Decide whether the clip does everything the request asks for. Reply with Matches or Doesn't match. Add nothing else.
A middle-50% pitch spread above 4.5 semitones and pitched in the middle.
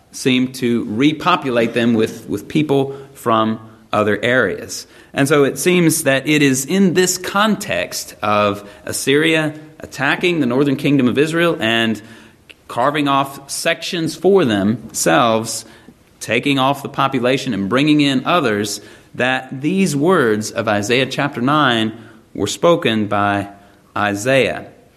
Doesn't match